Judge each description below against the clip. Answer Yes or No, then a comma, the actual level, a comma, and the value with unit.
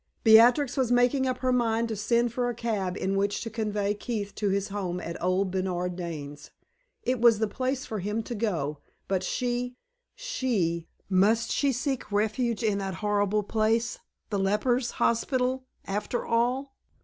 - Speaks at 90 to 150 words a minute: No, average, 165 wpm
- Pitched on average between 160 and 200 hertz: No, high, 220 Hz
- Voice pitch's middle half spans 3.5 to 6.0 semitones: Yes, average, 3.8 semitones